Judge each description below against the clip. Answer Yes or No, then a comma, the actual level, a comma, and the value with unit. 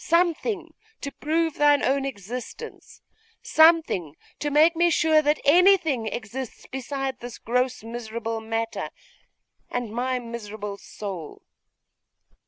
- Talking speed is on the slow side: Yes, slow, 110 wpm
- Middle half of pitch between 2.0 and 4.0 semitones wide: No, wide, 5.6 semitones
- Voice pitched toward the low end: No, very high, 260 Hz